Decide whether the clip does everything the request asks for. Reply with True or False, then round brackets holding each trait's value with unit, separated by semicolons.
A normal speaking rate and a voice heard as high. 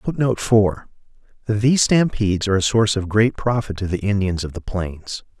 False (180 wpm; 105 Hz)